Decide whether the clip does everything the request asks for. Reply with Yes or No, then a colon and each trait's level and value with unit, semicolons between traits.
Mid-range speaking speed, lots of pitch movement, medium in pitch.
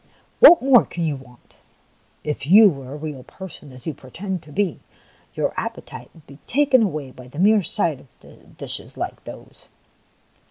Yes: average, 170 wpm; wide, 6.8 semitones; medium, 160 Hz